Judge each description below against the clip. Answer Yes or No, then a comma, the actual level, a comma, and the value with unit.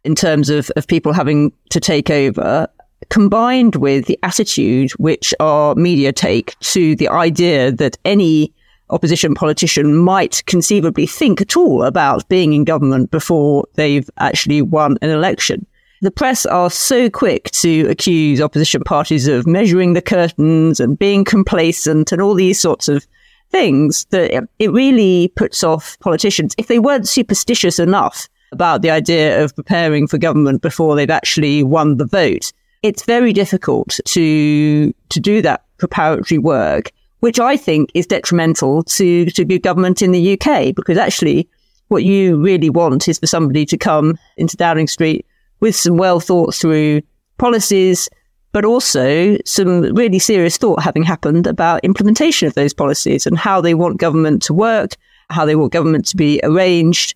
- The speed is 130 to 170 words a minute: Yes, average, 160 wpm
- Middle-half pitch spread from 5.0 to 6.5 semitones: No, average, 4.2 semitones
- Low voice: No, medium, 170 Hz